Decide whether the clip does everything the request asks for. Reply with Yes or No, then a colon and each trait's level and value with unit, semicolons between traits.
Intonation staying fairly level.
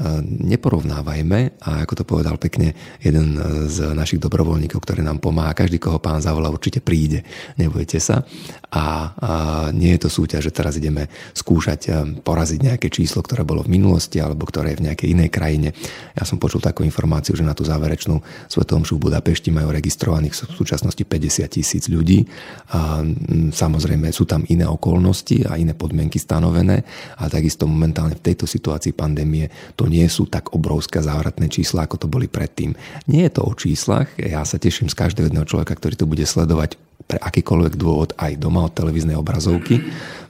Yes: narrow, 2.2 semitones